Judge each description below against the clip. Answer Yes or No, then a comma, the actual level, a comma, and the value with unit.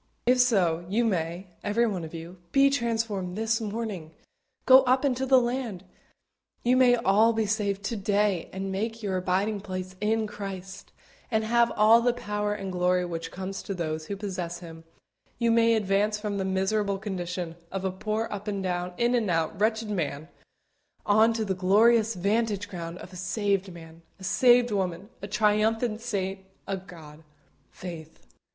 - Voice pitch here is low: No, high, 200 Hz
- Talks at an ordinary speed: Yes, average, 170 wpm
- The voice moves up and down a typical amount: Yes, average, 3.5 semitones